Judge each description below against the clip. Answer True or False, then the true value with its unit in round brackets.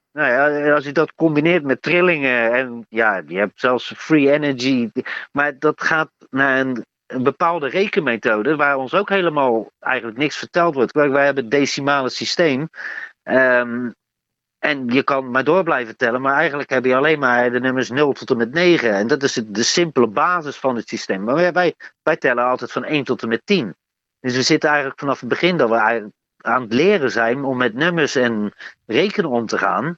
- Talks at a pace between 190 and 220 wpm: True (200 wpm)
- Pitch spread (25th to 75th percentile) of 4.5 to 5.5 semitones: False (3.6 semitones)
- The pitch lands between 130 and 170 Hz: True (135 Hz)